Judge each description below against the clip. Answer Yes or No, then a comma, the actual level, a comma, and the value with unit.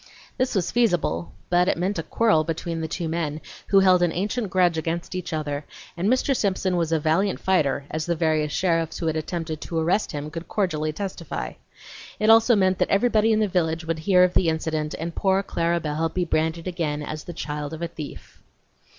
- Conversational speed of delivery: No, fast, 210 wpm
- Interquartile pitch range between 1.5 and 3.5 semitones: Yes, average, 3.1 semitones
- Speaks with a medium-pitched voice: Yes, medium, 170 Hz